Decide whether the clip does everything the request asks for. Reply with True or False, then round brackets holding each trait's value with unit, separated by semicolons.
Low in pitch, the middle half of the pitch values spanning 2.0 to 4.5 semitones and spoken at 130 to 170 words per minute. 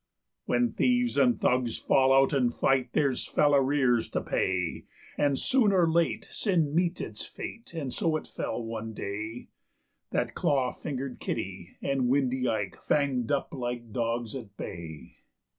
True (130 Hz; 4.1 semitones; 155 wpm)